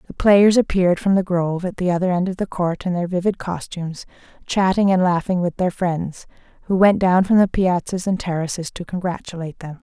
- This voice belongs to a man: No, female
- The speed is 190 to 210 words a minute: Yes, fast, 205 wpm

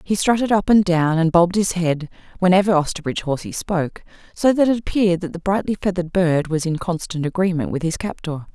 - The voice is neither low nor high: Yes, medium, 180 Hz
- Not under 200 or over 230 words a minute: Yes, fast, 205 wpm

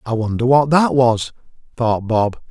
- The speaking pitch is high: No, low, 120 Hz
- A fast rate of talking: No, average, 165 wpm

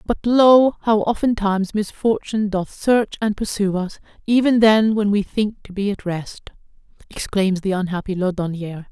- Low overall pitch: No, high, 205 Hz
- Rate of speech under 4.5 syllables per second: No, 4.9 syllables/s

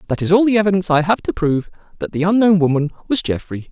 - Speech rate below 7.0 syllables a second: No, 7.3 syllables/s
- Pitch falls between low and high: Yes, medium, 175 Hz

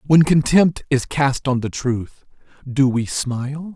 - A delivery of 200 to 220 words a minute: No, average, 160 wpm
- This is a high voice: No, medium, 140 Hz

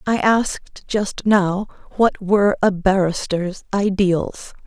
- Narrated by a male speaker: No, female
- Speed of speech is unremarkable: No, slow, 115 wpm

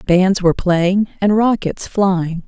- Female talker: Yes, female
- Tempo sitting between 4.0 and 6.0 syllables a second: No, 3.7 syllables/s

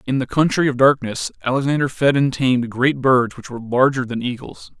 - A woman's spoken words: No, male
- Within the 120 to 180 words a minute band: No, average, 200 wpm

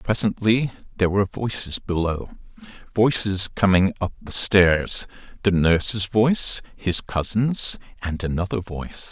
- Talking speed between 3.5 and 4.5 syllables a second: Yes, 4.4 syllables/s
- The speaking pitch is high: No, low, 100 Hz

